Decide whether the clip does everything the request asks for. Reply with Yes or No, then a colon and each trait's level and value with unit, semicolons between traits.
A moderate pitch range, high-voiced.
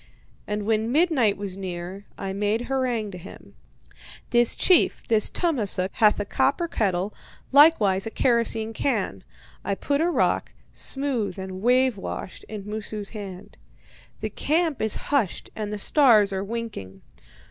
Yes: average, 4.3 semitones; high, 215 Hz